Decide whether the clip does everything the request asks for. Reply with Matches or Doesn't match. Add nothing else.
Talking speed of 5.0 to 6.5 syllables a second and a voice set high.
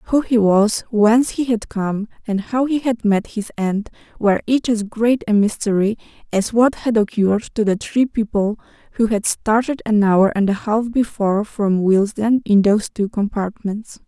Doesn't match